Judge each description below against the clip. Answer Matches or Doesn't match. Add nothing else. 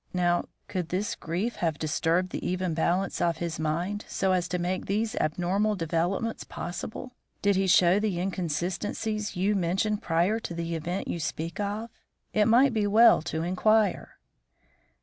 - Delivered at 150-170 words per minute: Matches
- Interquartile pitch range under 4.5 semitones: Matches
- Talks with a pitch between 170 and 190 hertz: Matches